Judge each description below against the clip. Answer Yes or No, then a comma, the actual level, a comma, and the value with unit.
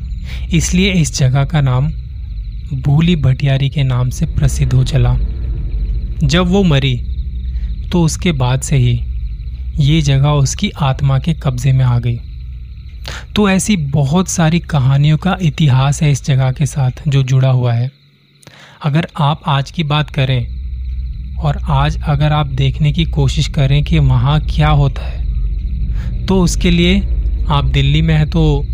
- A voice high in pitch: No, low, 135 Hz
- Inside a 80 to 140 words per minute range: No, average, 150 wpm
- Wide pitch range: Yes, wide, 6.9 semitones